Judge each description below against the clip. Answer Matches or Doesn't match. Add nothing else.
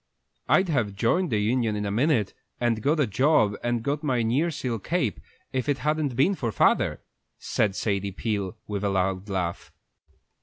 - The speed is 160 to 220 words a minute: Matches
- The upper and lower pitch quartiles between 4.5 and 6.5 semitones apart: Matches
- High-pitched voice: Doesn't match